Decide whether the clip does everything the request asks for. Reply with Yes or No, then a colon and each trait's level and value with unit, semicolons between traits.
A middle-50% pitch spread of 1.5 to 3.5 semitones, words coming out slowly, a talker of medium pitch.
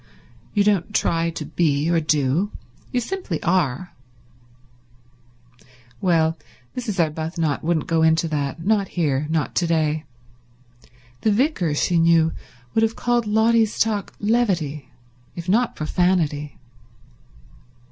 No: average, 5.0 semitones; slow, 115 wpm; medium, 170 Hz